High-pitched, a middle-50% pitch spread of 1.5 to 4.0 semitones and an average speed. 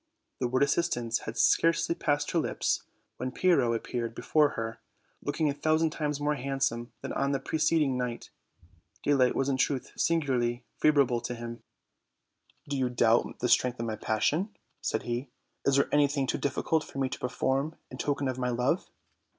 No: low, 135 Hz; average, 3.3 semitones; average, 175 wpm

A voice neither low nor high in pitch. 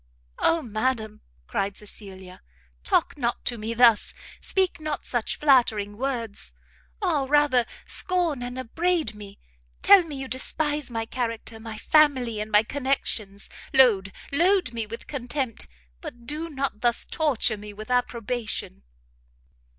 No: high, 245 Hz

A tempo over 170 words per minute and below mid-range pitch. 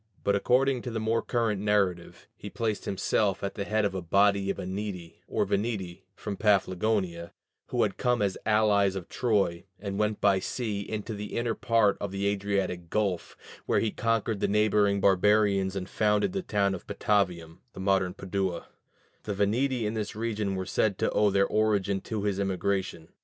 Yes: average, 180 wpm; low, 100 Hz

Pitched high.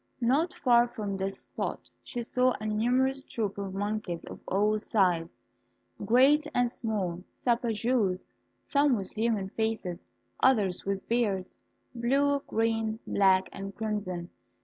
Yes: high, 220 Hz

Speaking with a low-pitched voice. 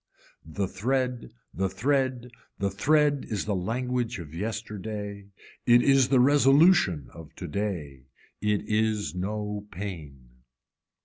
Yes: low, 105 Hz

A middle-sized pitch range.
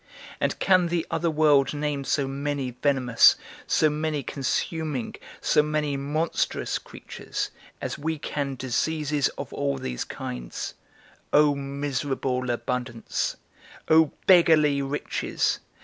No: narrow, 2.2 semitones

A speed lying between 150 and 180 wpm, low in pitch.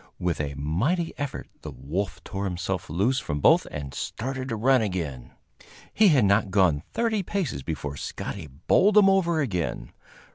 Yes: average, 160 wpm; low, 100 Hz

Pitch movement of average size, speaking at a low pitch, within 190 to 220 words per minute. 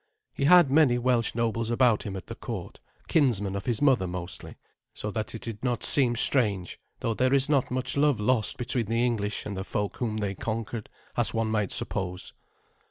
Yes: average, 3.6 semitones; low, 115 Hz; average, 195 wpm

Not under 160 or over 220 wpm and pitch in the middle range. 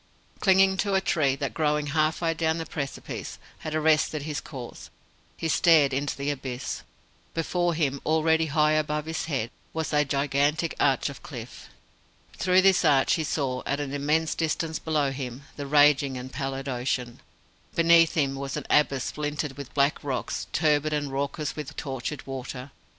Yes: average, 165 wpm; medium, 150 Hz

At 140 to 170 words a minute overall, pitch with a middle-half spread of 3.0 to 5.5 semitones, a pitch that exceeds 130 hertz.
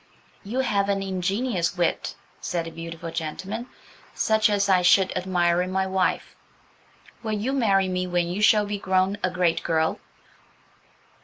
No: average, 155 wpm; narrow, 2.6 semitones; high, 190 Hz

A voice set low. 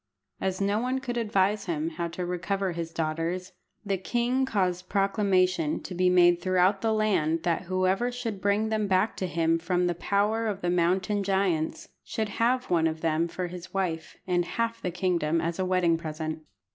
No: medium, 185 Hz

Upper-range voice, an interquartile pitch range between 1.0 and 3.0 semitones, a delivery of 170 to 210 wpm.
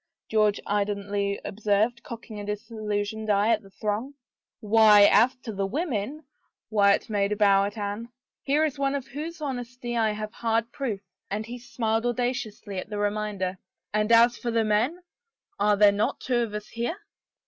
Yes: high, 215 Hz; average, 2.7 semitones; average, 195 wpm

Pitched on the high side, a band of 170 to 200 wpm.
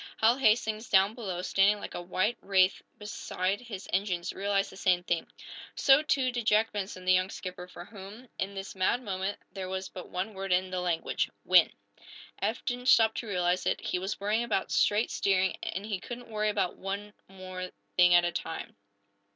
Yes: high, 195 Hz; average, 195 wpm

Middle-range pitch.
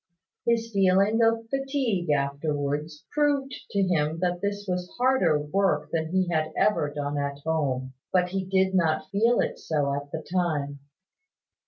Yes: medium, 180 Hz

